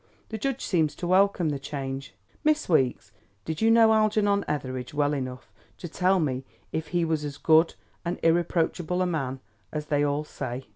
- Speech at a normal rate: Yes, average, 180 wpm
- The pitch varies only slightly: No, average, 4.5 semitones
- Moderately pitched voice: Yes, medium, 160 Hz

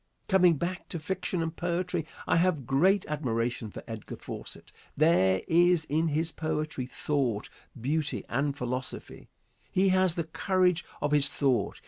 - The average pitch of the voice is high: No, medium, 155 Hz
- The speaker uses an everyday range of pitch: Yes, average, 4.6 semitones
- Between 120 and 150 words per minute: Yes, average, 145 wpm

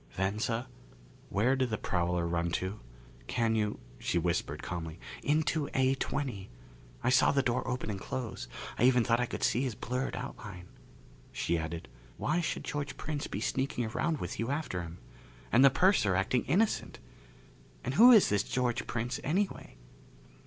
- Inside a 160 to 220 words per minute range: Yes, average, 165 wpm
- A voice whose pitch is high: No, low, 120 Hz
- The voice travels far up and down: Yes, wide, 5.8 semitones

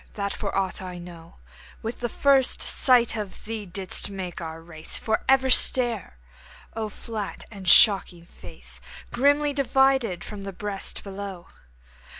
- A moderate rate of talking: Yes, average, 145 wpm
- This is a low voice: No, high, 205 Hz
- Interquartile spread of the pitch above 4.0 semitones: Yes, average, 4.6 semitones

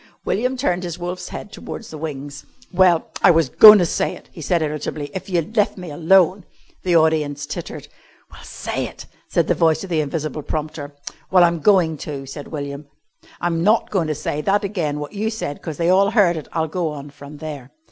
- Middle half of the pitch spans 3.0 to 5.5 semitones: Yes, average, 3.8 semitones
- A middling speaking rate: No, fast, 210 wpm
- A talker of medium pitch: Yes, medium, 160 Hz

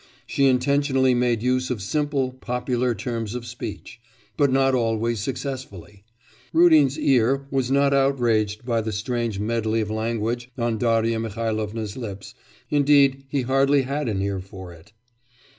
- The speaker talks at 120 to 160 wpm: Yes, average, 140 wpm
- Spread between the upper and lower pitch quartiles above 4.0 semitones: No, average, 3.5 semitones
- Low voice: Yes, low, 120 Hz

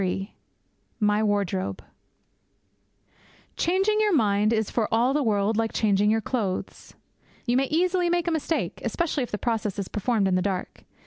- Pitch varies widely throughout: Yes, wide, 6.6 semitones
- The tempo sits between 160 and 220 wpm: Yes, average, 165 wpm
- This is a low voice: No, high, 220 Hz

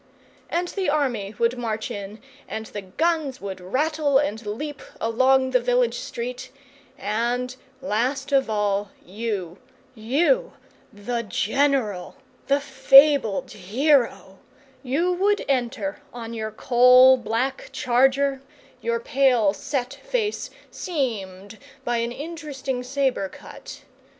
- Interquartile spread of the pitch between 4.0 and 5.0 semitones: Yes, average, 4.3 semitones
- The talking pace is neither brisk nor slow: No, slow, 115 wpm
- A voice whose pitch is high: Yes, very high, 250 Hz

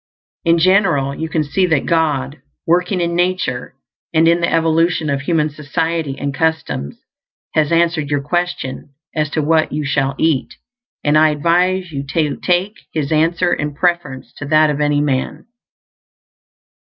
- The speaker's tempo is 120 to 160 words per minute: Yes, average, 155 wpm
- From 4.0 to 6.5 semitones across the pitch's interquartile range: No, average, 2.9 semitones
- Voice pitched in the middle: Yes, medium, 155 Hz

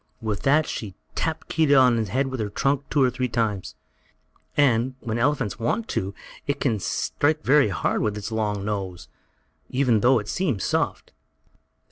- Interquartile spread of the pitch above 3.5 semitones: Yes, average, 4.9 semitones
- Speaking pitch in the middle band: No, low, 120 Hz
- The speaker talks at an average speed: Yes, average, 175 wpm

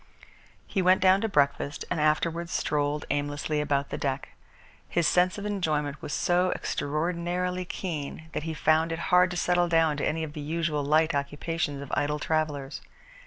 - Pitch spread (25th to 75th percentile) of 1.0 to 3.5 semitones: Yes, average, 3.2 semitones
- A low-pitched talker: No, medium, 160 Hz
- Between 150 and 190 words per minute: Yes, average, 170 wpm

